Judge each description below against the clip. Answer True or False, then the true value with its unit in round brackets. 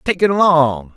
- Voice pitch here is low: False (155 Hz)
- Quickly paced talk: False (190 wpm)